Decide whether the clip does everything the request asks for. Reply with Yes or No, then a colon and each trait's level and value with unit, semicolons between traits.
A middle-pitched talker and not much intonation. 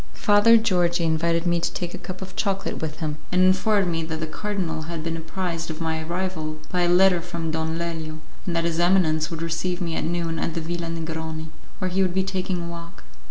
Yes: medium, 170 Hz; narrow, 2.2 semitones